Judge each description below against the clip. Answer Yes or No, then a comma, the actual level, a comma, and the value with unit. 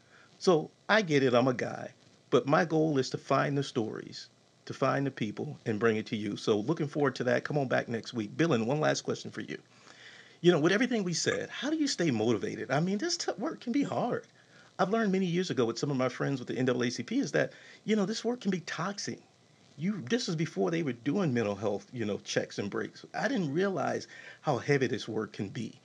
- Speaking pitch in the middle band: Yes, medium, 155 Hz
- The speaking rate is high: Yes, fast, 245 wpm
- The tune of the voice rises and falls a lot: Yes, wide, 7.5 semitones